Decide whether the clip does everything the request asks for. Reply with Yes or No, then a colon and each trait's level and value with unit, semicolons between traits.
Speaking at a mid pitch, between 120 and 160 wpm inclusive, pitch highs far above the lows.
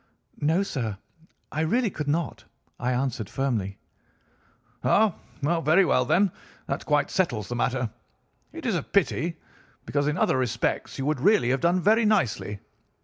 Yes: medium, 145 Hz; average, 150 wpm; wide, 6.2 semitones